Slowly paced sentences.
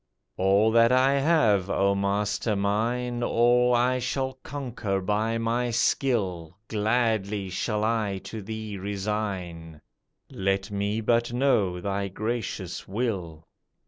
Yes: slow, 115 wpm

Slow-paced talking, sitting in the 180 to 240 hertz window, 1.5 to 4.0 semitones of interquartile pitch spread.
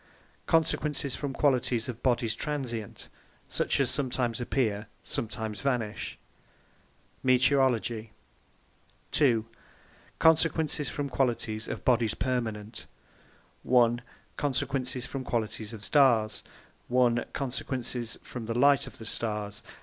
No: slow, 115 wpm; low, 125 Hz; average, 3.2 semitones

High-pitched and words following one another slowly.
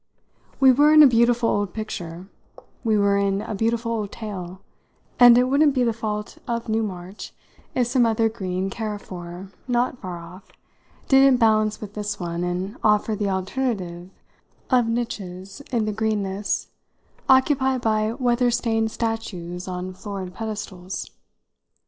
No: high, 215 Hz; average, 145 wpm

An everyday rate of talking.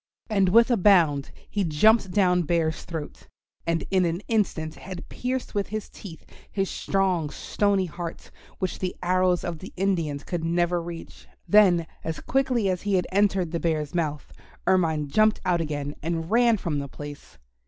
Yes: average, 170 wpm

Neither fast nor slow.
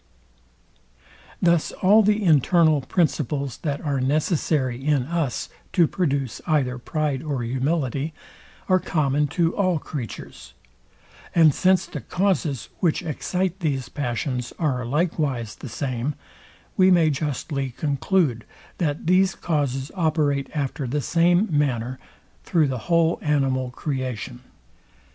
No: slow, 120 wpm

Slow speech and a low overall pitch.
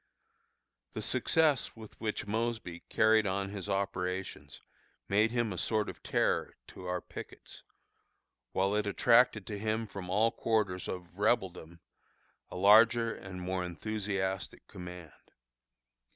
Yes: slow, 125 wpm; low, 100 Hz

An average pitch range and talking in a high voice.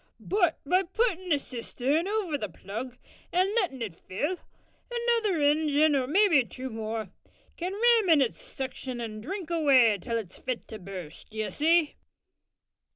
No: wide, 8.0 semitones; very high, 290 Hz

